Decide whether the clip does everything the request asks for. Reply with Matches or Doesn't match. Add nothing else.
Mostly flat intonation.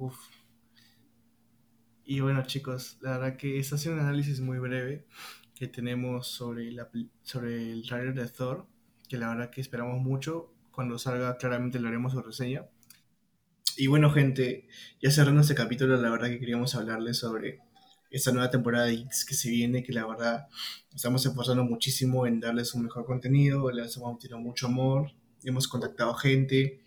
Matches